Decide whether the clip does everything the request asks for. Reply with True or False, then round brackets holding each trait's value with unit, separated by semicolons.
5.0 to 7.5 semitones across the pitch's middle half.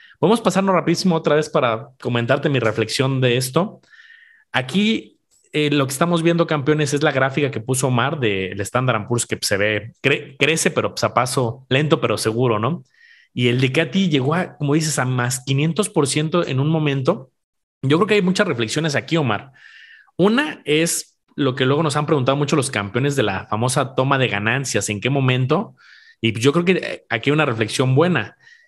False (4.6 semitones)